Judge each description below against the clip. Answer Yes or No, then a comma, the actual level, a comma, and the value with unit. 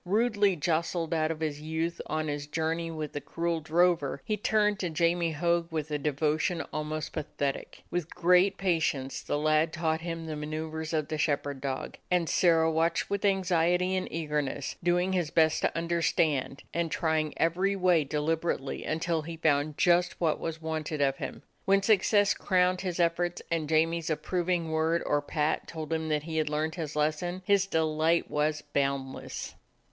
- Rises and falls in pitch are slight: Yes, narrow, 2.3 semitones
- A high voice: No, medium, 160 Hz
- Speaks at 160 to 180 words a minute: Yes, average, 170 wpm